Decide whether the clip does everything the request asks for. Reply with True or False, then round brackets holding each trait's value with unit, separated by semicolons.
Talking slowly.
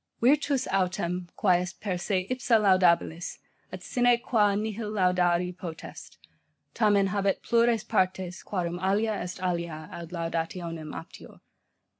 True (125 wpm)